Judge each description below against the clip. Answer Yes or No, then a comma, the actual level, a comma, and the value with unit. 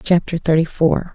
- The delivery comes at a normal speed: Yes, average, 155 wpm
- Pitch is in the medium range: Yes, medium, 165 Hz